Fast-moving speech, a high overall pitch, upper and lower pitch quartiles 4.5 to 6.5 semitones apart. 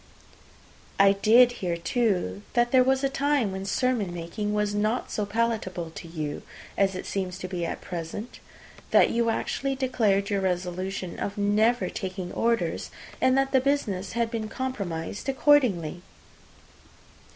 No: average, 150 wpm; high, 205 Hz; average, 4.9 semitones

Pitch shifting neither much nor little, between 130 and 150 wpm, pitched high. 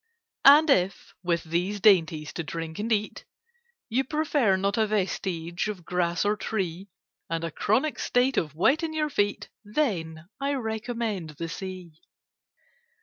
No: wide, 5.7 semitones; average, 145 wpm; high, 200 Hz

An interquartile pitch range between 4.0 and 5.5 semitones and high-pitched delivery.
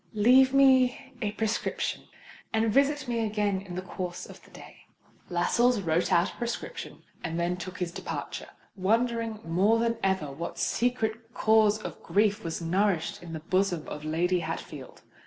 Yes: average, 4.6 semitones; high, 205 Hz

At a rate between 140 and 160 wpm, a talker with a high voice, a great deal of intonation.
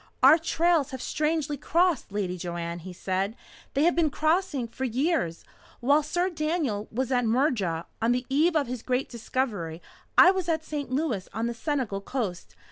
No: average, 175 wpm; very high, 260 Hz; wide, 6.8 semitones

